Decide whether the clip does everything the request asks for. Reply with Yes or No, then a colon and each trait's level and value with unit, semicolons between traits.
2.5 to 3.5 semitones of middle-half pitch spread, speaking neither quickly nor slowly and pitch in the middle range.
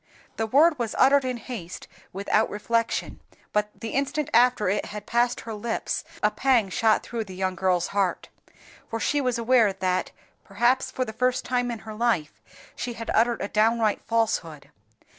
No: average, 3.1 semitones; average, 175 wpm; high, 225 Hz